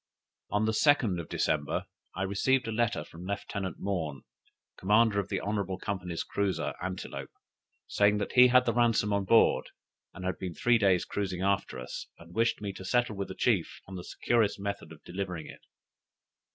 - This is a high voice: No, low, 100 Hz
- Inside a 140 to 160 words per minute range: No, average, 180 wpm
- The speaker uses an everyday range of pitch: Yes, average, 3.2 semitones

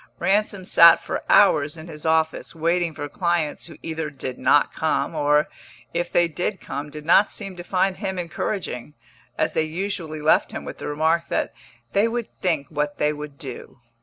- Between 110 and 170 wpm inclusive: No, average, 185 wpm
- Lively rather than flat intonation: No, average, 3.1 semitones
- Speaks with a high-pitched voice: No, medium, 160 Hz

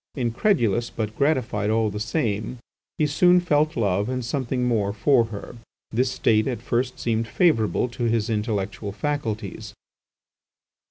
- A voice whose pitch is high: No, low, 115 Hz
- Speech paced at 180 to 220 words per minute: No, average, 140 wpm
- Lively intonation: No, average, 3.5 semitones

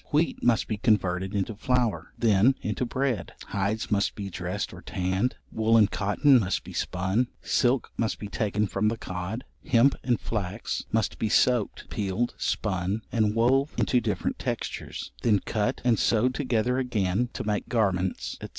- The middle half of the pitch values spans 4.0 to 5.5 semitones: No, average, 3.6 semitones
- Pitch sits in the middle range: No, low, 110 Hz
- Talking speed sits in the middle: Yes, average, 165 wpm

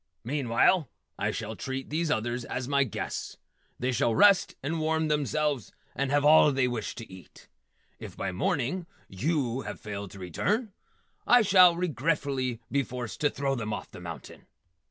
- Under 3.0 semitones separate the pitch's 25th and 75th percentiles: No, average, 4.8 semitones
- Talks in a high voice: No, low, 135 Hz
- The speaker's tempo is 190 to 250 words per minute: No, average, 165 wpm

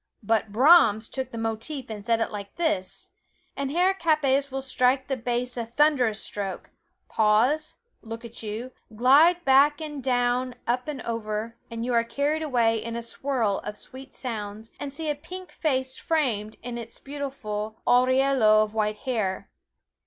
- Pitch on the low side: No, high, 245 Hz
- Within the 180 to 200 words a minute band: No, average, 165 wpm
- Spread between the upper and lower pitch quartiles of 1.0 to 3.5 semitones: No, average, 4.0 semitones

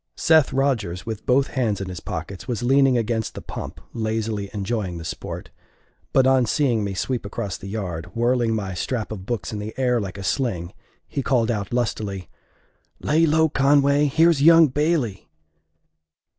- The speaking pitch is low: Yes, low, 115 Hz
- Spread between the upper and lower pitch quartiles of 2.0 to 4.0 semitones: No, average, 5.1 semitones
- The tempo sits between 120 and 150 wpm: No, average, 170 wpm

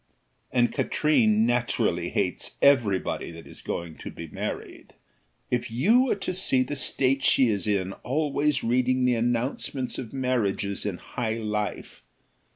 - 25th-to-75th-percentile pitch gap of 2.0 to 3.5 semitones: No, average, 3.9 semitones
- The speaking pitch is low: Yes, low, 120 Hz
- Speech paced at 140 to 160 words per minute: Yes, average, 150 wpm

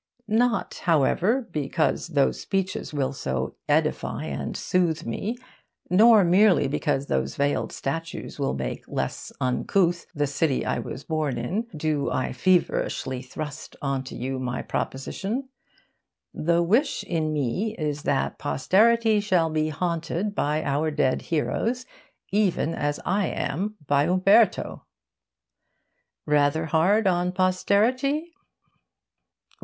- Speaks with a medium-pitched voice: Yes, medium, 165 Hz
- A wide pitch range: Yes, wide, 5.7 semitones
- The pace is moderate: No, slow, 120 wpm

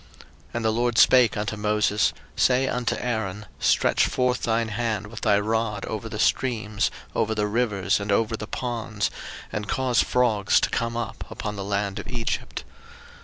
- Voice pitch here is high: No, low, 110 Hz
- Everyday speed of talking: Yes, average, 170 wpm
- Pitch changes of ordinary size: No, narrow, 2.2 semitones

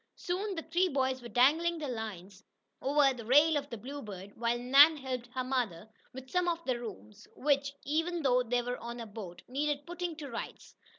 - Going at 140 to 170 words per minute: No, average, 195 wpm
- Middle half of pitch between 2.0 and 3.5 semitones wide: No, average, 4.3 semitones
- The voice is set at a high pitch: Yes, very high, 260 Hz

